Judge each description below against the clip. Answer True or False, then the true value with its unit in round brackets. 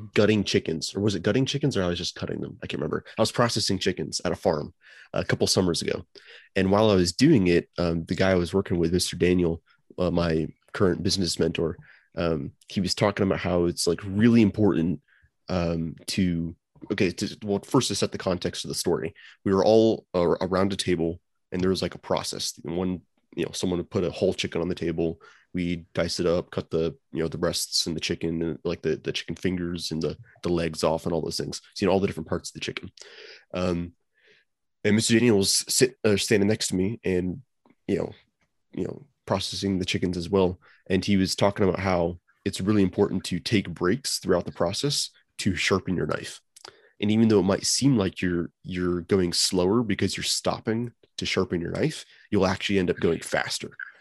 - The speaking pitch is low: True (90 Hz)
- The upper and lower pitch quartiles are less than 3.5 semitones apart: True (2.8 semitones)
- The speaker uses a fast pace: True (215 wpm)